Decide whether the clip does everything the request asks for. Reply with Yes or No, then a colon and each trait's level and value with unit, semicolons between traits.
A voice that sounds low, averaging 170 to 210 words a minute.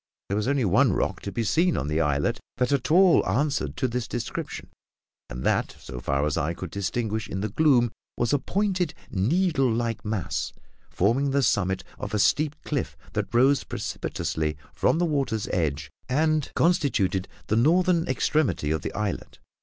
Yes: low, 120 Hz; average, 175 wpm